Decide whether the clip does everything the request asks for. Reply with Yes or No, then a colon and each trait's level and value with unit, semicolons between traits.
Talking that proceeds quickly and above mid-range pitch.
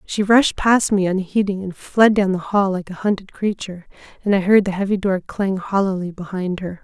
Yes: fast, 210 wpm; high, 195 Hz